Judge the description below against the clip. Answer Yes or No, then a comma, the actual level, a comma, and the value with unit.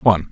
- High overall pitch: No, very low, 90 Hz